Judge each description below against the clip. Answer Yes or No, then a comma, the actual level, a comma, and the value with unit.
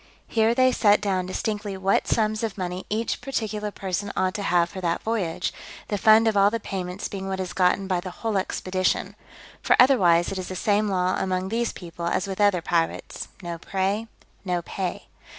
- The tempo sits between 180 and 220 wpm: Yes, average, 195 wpm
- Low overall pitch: No, high, 195 Hz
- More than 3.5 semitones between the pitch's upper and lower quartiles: No, average, 2.7 semitones